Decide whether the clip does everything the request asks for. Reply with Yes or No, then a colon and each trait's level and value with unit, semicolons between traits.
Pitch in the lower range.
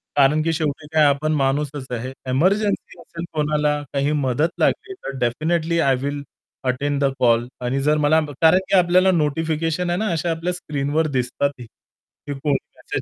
No: medium, 150 Hz